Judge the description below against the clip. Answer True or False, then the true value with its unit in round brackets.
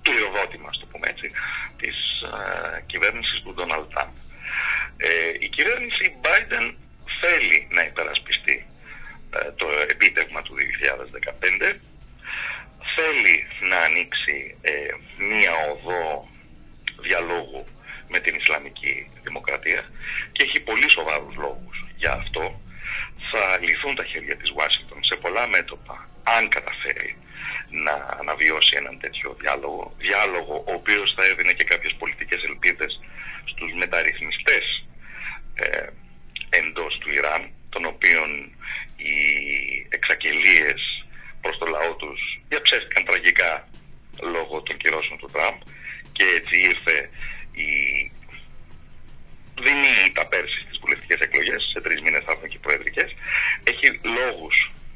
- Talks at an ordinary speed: False (110 wpm)